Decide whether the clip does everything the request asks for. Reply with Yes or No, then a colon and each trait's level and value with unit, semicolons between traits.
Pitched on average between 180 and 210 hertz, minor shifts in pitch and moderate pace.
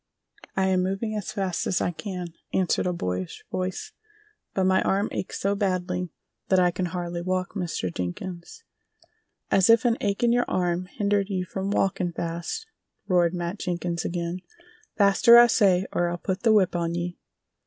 Yes: medium, 185 Hz; narrow, 2.2 semitones; average, 175 wpm